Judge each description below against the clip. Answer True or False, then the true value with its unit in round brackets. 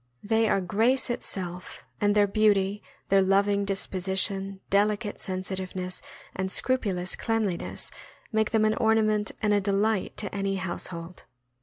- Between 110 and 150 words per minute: True (140 wpm)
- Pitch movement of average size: False (2.1 semitones)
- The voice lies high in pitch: True (200 Hz)